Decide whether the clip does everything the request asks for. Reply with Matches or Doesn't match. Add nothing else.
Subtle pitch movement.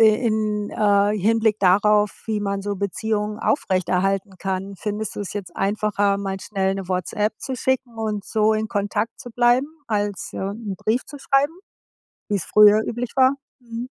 Matches